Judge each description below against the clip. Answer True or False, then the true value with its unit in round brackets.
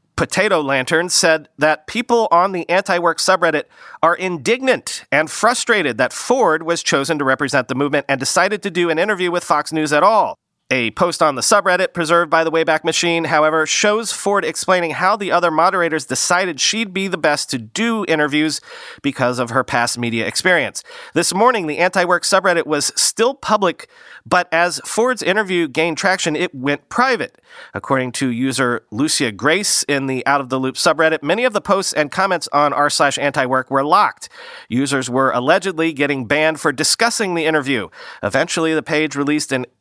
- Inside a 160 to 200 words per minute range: True (180 wpm)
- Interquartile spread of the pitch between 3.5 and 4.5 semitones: True (4.1 semitones)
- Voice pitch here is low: False (160 Hz)